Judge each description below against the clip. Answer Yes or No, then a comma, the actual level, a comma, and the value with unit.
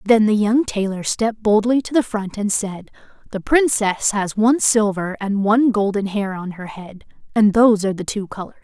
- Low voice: No, high, 210 Hz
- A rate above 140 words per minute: Yes, average, 200 wpm